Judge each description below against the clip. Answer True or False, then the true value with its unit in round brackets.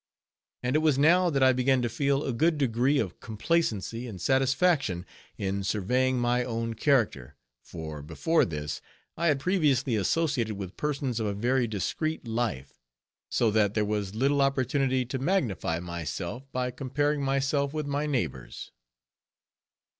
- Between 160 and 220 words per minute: False (150 wpm)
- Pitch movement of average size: True (4.9 semitones)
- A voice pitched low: True (125 Hz)